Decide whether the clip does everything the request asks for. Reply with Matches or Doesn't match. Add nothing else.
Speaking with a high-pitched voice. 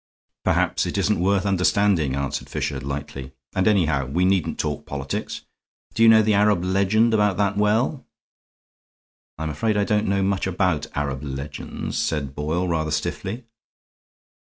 Doesn't match